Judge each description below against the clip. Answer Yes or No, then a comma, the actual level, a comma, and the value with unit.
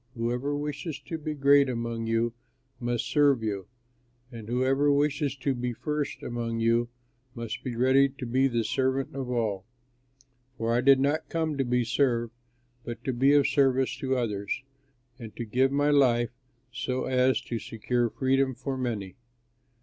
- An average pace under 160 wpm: No, average, 165 wpm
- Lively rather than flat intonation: No, average, 2.8 semitones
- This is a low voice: Yes, low, 130 Hz